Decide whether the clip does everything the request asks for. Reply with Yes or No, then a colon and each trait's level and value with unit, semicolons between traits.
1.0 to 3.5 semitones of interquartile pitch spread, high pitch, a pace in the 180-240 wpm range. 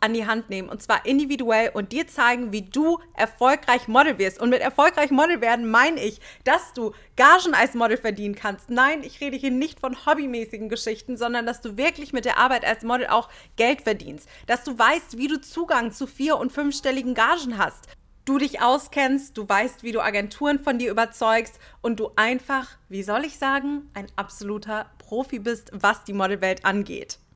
No: average, 4.0 semitones; high, 240 Hz; fast, 190 wpm